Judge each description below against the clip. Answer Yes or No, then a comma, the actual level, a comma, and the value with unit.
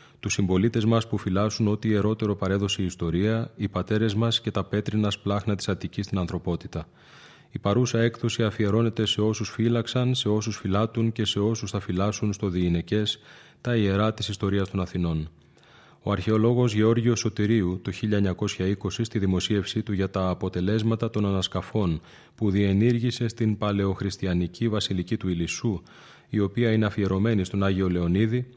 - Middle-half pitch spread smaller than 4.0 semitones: Yes, average, 2.8 semitones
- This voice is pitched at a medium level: No, low, 105 Hz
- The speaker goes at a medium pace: Yes, average, 150 wpm